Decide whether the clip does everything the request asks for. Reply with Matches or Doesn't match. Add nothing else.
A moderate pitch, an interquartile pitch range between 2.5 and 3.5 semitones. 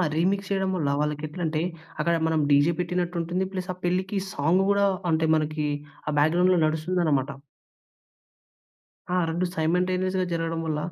Matches